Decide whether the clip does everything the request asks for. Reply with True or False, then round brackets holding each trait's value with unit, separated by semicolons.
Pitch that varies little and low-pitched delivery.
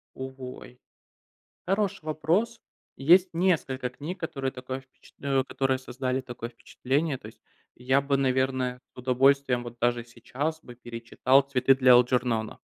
True (2.0 semitones; 130 Hz)